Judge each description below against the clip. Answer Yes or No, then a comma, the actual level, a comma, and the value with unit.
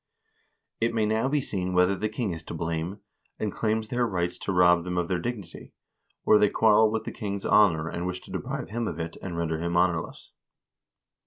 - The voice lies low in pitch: Yes, very low, 95 Hz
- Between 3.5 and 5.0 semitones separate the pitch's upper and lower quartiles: Yes, average, 4.0 semitones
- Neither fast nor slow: No, fast, 215 wpm